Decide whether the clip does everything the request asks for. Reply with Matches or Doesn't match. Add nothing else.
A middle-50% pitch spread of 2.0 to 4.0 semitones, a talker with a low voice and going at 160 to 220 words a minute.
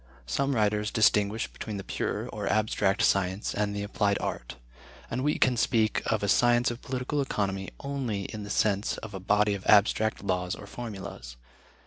Matches